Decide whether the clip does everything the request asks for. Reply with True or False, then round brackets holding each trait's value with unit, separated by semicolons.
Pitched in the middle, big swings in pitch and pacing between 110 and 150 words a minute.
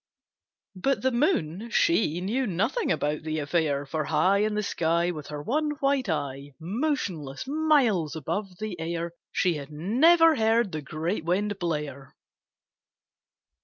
True (180 Hz; 7.3 semitones; 140 wpm)